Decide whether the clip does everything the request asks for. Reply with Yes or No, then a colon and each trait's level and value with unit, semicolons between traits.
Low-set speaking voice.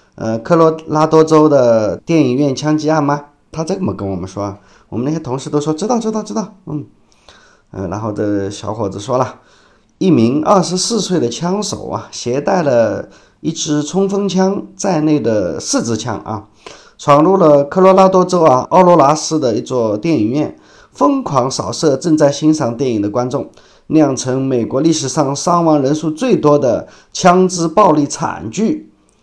No: medium, 150 Hz